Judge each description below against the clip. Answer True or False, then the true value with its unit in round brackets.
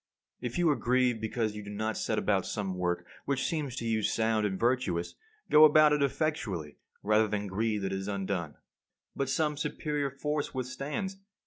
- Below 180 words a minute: False (185 wpm)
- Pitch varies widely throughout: True (5.7 semitones)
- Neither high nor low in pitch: False (115 Hz)